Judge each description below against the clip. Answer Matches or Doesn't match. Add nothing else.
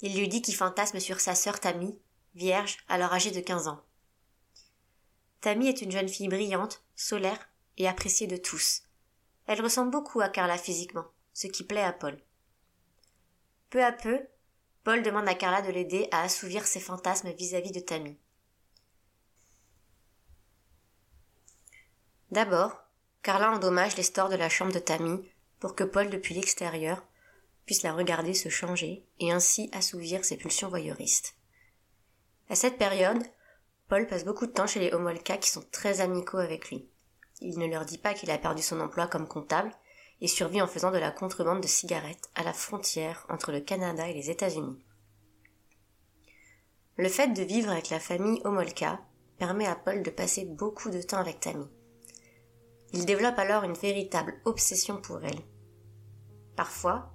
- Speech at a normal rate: Matches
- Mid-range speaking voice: Matches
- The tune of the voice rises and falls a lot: Matches